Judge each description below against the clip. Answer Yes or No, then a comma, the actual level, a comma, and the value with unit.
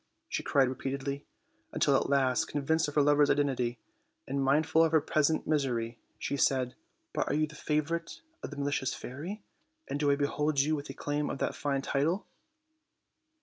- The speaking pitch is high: No, medium, 145 Hz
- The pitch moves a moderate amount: No, narrow, 2.0 semitones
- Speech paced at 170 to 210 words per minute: Yes, average, 185 wpm